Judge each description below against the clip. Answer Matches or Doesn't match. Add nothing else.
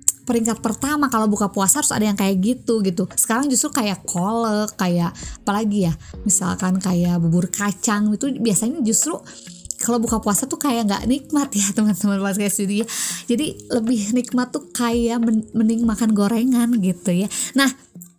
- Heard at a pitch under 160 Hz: Doesn't match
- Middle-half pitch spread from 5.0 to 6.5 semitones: Doesn't match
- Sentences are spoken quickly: Matches